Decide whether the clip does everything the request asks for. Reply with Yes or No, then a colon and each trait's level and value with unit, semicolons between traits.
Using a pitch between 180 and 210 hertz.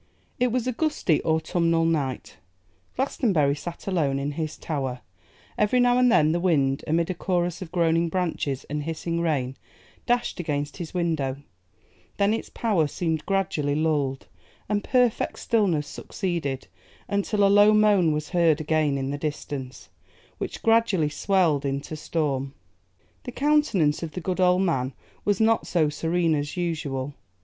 No: medium, 165 Hz